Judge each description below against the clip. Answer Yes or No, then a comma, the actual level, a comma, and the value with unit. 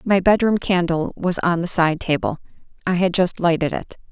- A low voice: No, medium, 175 Hz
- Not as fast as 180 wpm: No, average, 190 wpm